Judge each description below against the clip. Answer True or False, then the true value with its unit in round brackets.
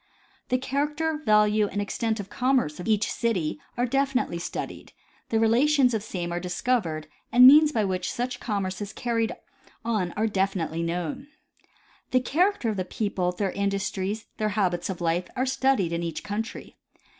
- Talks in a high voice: True (210 Hz)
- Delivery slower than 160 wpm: False (170 wpm)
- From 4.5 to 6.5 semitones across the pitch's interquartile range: True (5.3 semitones)